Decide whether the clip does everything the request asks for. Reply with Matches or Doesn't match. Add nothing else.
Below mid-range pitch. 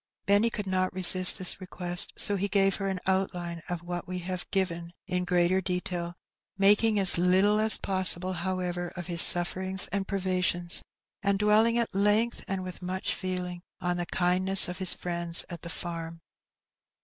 Doesn't match